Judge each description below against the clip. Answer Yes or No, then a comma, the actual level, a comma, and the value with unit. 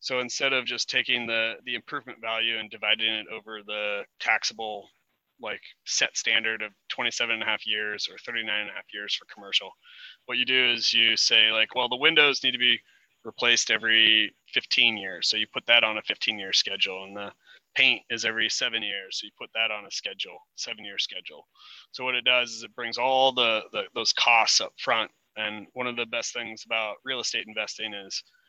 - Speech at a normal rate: No, fast, 210 wpm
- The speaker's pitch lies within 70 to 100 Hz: No, low, 115 Hz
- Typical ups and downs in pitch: No, narrow, 2.3 semitones